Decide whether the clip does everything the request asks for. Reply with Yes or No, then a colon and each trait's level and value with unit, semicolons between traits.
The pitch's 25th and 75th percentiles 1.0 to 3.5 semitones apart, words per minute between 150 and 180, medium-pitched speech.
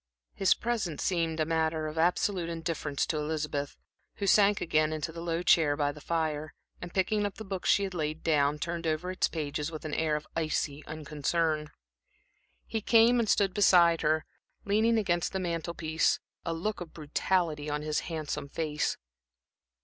Yes: average, 3.0 semitones; average, 175 wpm; medium, 165 Hz